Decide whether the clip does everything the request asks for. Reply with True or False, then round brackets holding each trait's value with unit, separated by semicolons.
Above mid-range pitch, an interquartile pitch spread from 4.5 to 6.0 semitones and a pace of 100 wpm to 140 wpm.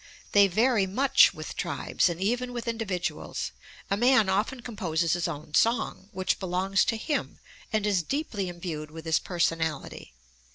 False (195 Hz; 5.0 semitones; 155 wpm)